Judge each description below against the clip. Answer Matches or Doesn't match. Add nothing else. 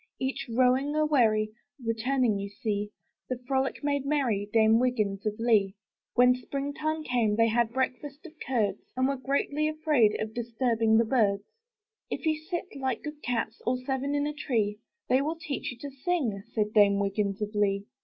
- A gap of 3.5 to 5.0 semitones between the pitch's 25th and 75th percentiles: Matches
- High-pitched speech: Matches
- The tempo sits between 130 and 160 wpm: Doesn't match